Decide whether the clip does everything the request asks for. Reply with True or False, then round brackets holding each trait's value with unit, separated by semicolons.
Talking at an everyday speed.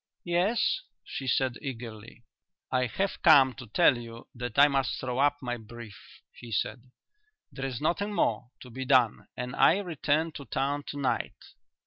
True (165 wpm)